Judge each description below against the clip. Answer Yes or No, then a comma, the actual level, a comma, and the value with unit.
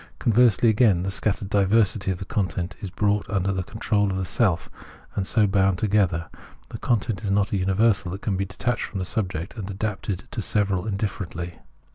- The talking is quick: No, average, 190 wpm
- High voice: No, low, 100 Hz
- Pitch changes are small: Yes, narrow, 2.1 semitones